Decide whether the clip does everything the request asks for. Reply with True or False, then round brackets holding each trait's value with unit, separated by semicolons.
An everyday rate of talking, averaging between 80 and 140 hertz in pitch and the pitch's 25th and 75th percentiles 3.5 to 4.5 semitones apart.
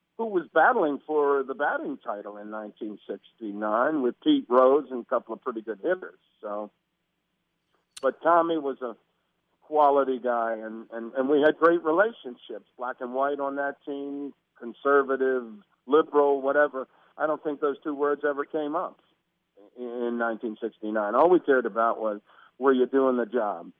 True (160 wpm; 135 Hz; 4.2 semitones)